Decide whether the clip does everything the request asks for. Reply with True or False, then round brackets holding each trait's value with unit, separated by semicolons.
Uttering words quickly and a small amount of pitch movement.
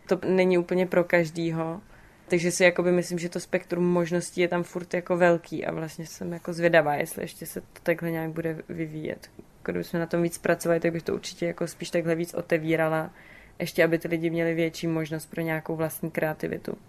True (195 wpm; 1.2 semitones)